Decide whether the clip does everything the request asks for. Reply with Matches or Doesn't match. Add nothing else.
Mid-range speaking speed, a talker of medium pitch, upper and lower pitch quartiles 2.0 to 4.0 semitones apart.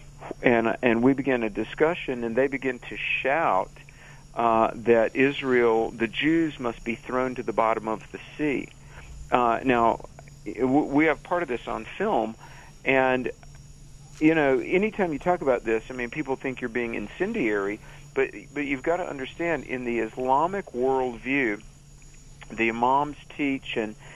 Doesn't match